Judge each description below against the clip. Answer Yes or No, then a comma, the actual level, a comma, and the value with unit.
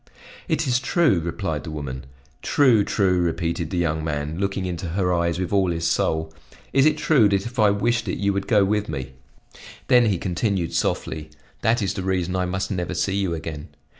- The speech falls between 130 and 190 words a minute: No, average, 200 wpm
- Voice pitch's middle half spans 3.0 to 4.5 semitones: Yes, average, 3.6 semitones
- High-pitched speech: No, very low, 95 Hz